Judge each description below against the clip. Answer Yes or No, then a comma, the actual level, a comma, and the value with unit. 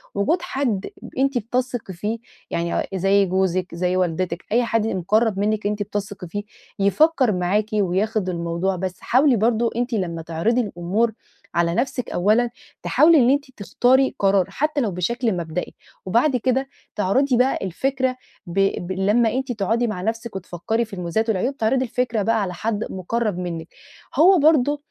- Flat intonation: No, average, 4.9 semitones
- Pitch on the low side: No, high, 215 Hz